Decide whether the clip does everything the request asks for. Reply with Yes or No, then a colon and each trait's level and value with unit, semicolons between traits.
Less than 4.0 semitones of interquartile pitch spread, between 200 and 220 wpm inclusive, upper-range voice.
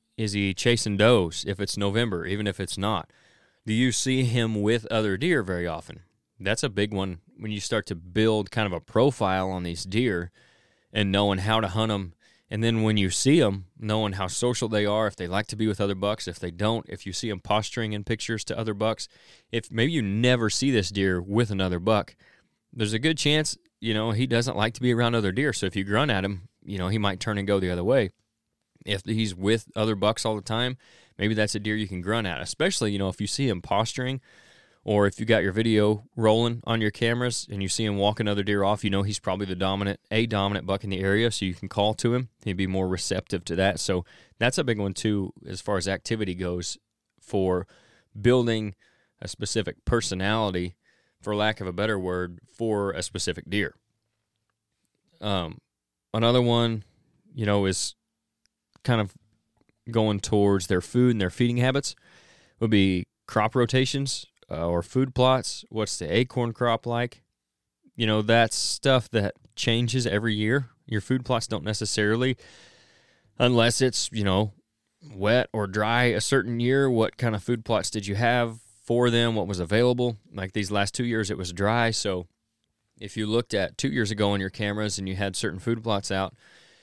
No: average, 2.9 semitones; fast, 205 wpm; low, 110 Hz